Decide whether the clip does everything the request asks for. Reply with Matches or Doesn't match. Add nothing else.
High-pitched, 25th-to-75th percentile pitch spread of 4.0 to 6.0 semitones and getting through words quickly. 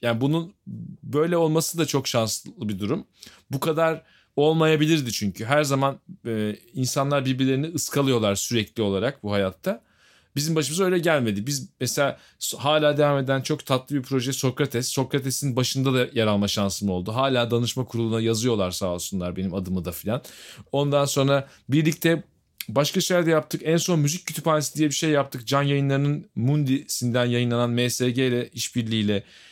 Doesn't match